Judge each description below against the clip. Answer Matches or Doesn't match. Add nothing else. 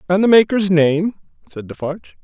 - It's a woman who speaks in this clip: Doesn't match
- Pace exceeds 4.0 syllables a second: Matches